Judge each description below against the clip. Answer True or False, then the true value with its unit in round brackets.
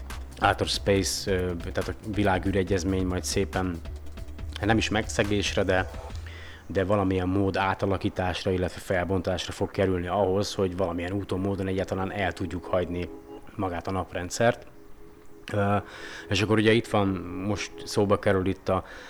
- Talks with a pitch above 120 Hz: False (95 Hz)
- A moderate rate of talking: True (130 wpm)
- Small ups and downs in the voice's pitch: True (2.3 semitones)